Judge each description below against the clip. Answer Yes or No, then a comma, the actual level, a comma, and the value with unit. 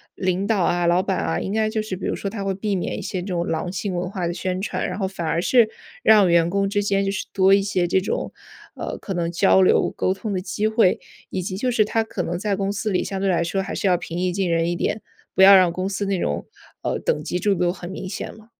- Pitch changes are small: Yes, narrow, 2.1 semitones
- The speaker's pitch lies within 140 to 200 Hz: Yes, high, 190 Hz